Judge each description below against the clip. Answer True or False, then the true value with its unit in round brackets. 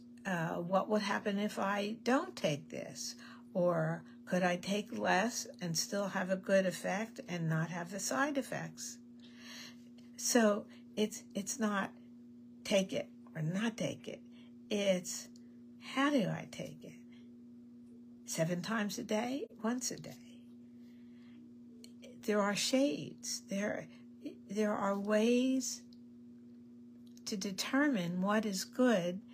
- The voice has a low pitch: False (235 Hz)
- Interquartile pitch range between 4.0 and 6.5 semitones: False (3.5 semitones)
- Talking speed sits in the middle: False (125 wpm)